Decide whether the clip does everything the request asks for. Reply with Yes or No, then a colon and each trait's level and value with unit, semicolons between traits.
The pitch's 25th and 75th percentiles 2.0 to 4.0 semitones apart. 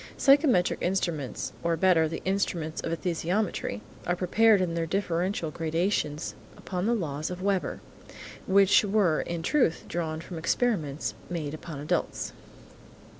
Yes: average, 3.3 semitones